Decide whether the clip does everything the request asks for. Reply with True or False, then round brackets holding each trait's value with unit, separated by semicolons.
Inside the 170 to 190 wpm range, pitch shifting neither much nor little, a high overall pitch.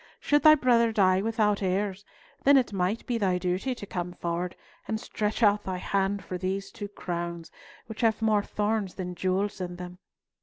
True (185 wpm; 3.2 semitones; 200 Hz)